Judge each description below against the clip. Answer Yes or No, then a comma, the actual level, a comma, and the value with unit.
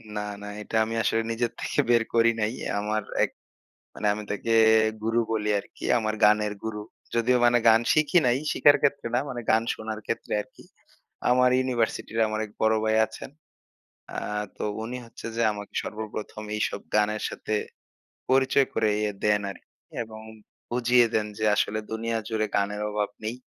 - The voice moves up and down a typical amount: No, narrow, 1.8 semitones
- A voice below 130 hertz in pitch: Yes, low, 110 Hz